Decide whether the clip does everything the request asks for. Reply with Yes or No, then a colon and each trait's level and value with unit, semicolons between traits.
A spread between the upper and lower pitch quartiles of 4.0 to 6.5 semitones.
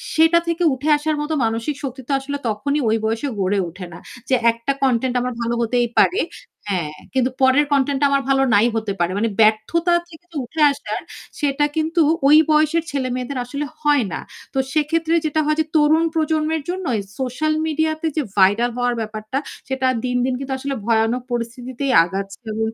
Yes: average, 4.8 semitones